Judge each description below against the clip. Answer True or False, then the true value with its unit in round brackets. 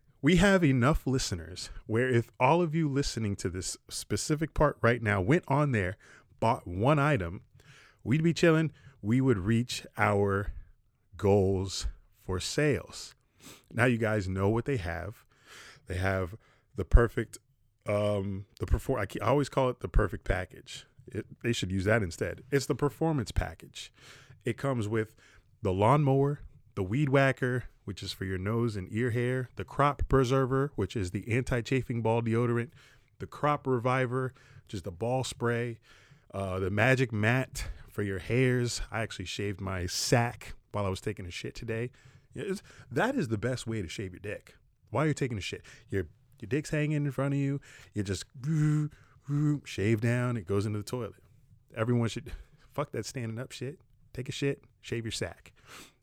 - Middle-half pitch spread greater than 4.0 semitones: True (4.6 semitones)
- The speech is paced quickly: False (175 wpm)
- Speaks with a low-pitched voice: True (120 Hz)